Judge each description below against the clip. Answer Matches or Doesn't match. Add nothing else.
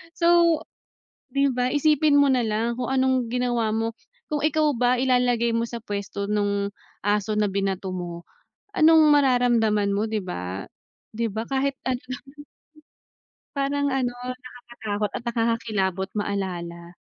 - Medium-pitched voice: Doesn't match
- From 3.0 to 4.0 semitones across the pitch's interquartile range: Doesn't match